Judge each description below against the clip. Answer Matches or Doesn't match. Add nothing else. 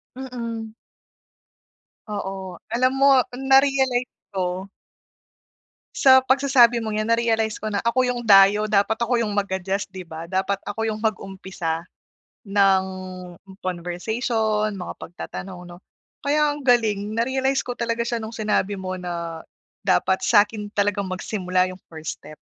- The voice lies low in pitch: Doesn't match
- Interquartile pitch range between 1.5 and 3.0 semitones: Doesn't match